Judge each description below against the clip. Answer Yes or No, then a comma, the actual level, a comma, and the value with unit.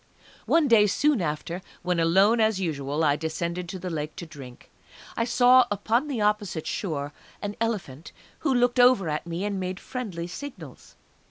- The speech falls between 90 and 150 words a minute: No, average, 170 wpm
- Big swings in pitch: Yes, wide, 6.0 semitones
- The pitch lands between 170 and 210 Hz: Yes, medium, 185 Hz